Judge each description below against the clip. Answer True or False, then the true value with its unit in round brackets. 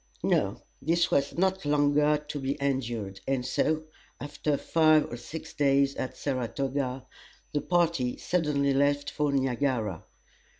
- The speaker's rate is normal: False (130 wpm)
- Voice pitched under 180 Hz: True (140 Hz)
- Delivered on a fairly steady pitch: True (2.1 semitones)